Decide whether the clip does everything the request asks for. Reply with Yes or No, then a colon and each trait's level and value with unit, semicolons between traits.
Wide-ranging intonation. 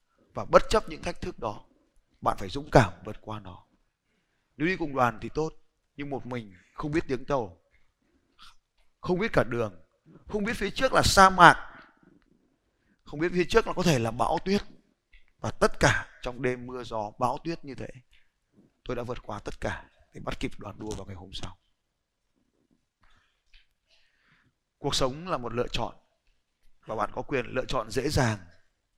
Yes: wide, 6.8 semitones